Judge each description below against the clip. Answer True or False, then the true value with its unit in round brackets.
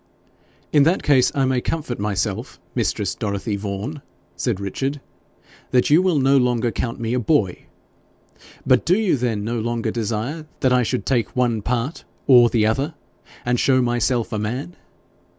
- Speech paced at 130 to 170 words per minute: True (165 wpm)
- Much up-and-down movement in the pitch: False (3.5 semitones)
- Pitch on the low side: True (125 Hz)